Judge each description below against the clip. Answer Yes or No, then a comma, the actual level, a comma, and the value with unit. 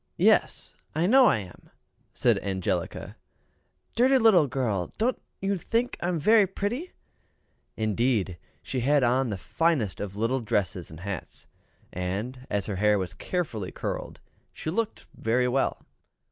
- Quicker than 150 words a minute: No, average, 145 wpm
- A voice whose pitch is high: No, low, 125 Hz